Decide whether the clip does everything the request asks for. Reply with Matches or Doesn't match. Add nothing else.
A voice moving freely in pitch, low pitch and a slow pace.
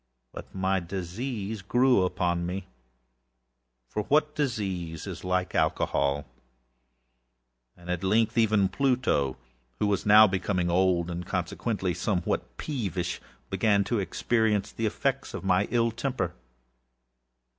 Matches